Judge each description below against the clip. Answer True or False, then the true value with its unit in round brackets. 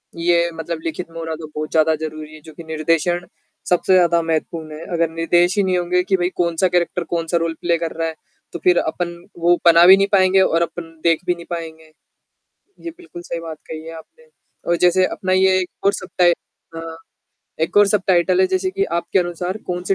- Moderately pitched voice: True (170 Hz)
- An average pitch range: False (1.7 semitones)